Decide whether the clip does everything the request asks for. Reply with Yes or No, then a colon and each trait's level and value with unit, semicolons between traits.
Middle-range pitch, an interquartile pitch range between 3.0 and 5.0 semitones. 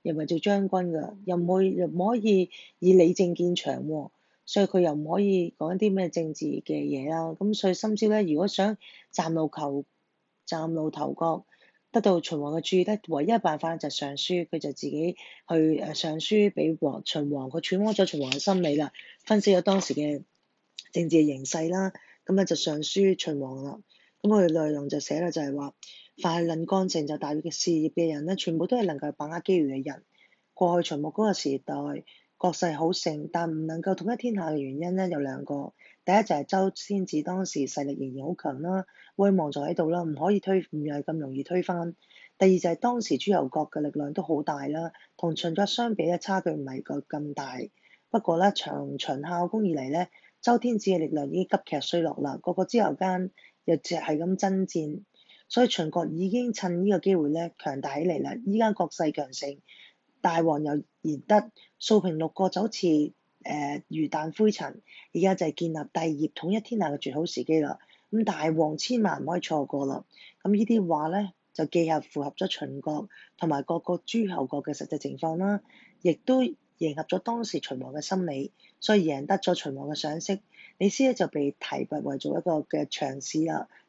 Yes: medium, 170 Hz; average, 4.0 semitones